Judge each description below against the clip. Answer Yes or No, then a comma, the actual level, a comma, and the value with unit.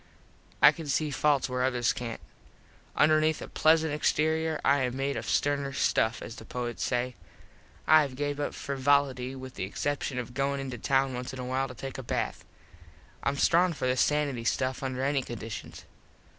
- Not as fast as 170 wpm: No, average, 185 wpm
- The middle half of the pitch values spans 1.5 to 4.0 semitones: Yes, narrow, 2.4 semitones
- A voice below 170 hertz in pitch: Yes, low, 135 Hz